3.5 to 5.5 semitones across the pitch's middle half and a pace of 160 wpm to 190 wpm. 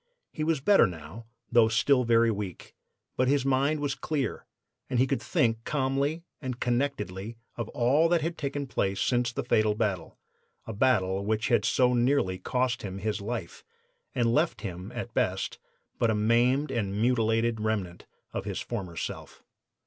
Yes: average, 4.1 semitones; average, 165 wpm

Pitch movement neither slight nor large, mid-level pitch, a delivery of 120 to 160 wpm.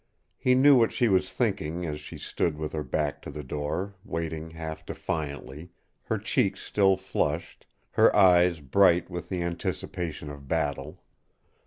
No: average, 3.8 semitones; very low, 85 Hz; average, 155 wpm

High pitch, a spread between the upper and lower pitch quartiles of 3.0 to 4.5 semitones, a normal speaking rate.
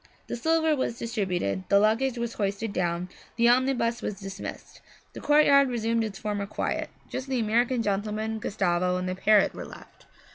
Yes: high, 220 Hz; average, 3.5 semitones; average, 170 wpm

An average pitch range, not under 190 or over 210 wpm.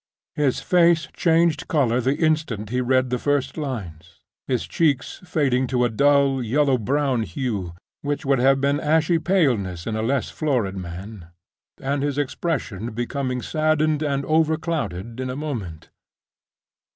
No: average, 4.6 semitones; average, 145 wpm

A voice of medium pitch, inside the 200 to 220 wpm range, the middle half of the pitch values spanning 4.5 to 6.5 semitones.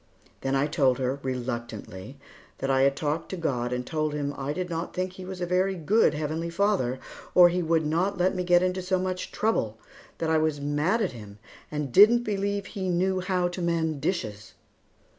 Yes: medium, 165 Hz; fast, 205 wpm; average, 5.2 semitones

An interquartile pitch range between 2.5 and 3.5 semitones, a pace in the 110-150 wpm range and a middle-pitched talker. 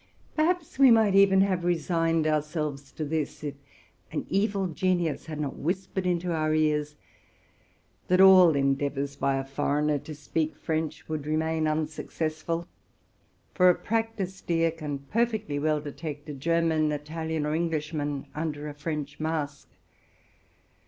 Yes: average, 2.9 semitones; average, 145 wpm; medium, 155 Hz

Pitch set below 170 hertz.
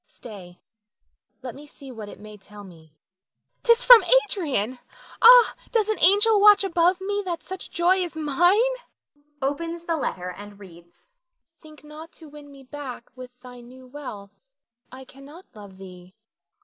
No: very high, 285 Hz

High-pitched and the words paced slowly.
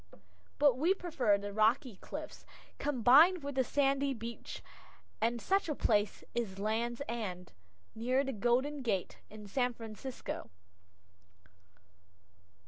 Yes: high, 240 Hz; slow, 120 wpm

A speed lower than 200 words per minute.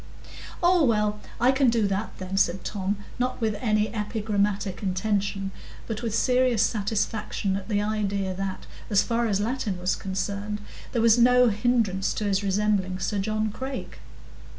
Yes: average, 155 wpm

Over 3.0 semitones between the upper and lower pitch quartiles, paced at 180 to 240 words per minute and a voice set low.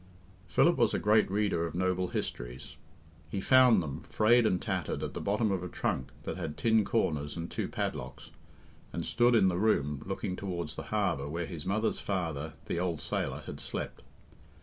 Yes: average, 4.7 semitones; average, 185 wpm; very low, 90 Hz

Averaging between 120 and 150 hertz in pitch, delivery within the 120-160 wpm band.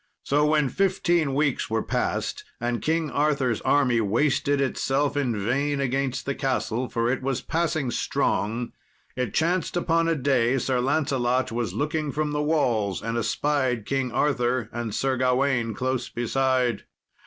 Yes: low, 135 Hz; average, 150 wpm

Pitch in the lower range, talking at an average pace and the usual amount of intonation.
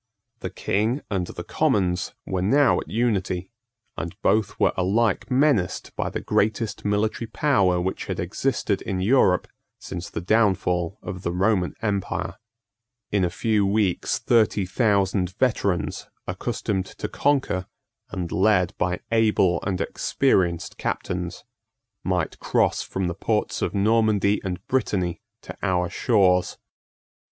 No: low, 100 Hz; slow, 130 wpm; average, 3.3 semitones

